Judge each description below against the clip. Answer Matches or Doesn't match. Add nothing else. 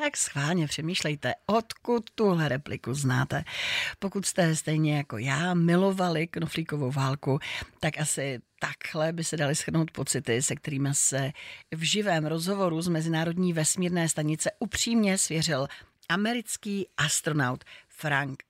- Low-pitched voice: Doesn't match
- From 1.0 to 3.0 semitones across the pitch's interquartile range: Doesn't match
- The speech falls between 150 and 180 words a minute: Doesn't match